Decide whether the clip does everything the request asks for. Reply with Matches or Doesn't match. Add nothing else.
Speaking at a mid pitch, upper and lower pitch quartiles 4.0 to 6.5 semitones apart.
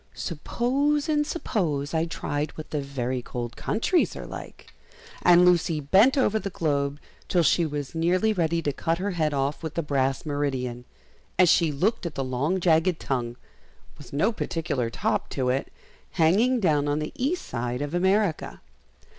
Matches